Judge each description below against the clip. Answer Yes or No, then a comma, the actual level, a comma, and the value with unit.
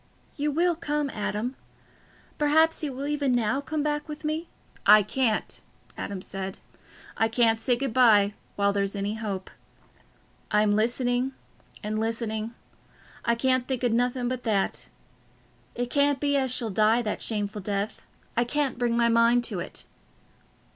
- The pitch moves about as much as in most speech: Yes, average, 4.2 semitones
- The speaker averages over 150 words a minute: No, average, 145 wpm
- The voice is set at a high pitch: Yes, high, 240 Hz